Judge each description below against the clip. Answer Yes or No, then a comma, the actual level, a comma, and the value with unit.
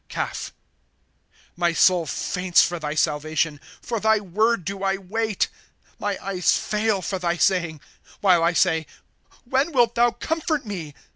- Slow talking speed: No, average, 155 wpm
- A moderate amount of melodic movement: Yes, average, 4.4 semitones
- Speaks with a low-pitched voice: No, high, 190 Hz